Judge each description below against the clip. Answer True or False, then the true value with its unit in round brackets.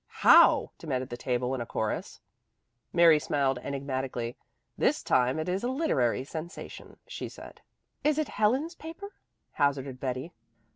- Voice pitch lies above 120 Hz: True (140 Hz)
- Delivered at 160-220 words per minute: False (140 wpm)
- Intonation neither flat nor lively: False (8.5 semitones)